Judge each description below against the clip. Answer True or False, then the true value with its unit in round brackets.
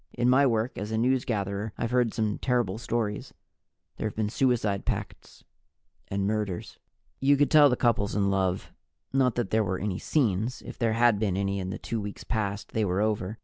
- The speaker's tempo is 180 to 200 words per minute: True (195 wpm)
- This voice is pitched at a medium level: False (110 Hz)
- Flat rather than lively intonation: False (3.3 semitones)